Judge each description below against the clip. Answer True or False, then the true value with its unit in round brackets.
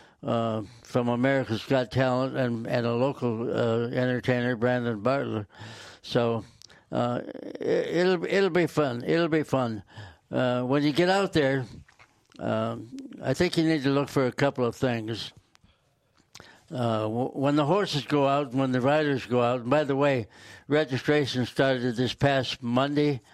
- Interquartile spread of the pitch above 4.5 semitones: False (3.4 semitones)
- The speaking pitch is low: True (125 Hz)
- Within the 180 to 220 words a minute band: False (160 wpm)